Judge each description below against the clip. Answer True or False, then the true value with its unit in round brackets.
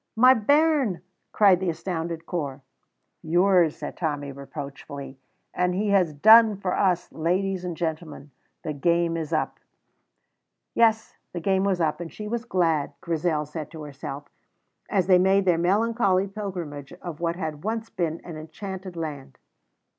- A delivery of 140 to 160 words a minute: True (150 wpm)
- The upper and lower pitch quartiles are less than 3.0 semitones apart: False (3.9 semitones)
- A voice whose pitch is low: False (175 Hz)